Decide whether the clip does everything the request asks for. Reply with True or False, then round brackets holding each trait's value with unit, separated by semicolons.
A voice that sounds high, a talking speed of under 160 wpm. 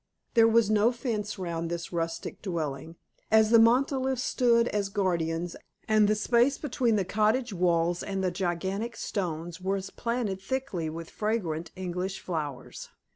True (195 Hz; 145 wpm)